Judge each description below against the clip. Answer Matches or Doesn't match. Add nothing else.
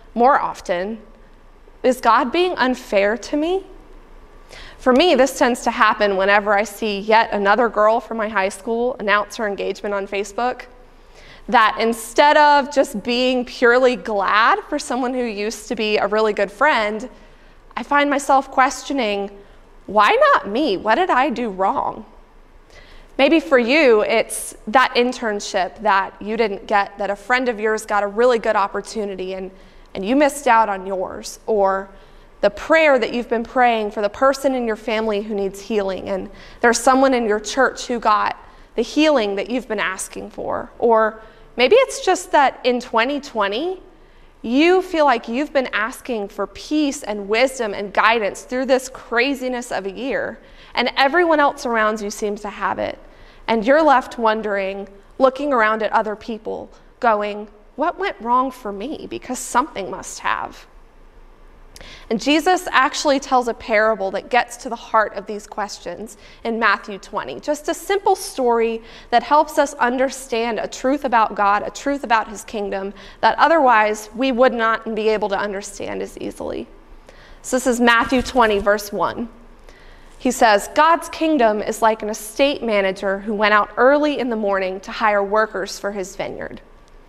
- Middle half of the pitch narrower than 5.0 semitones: Matches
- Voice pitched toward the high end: Matches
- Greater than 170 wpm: Doesn't match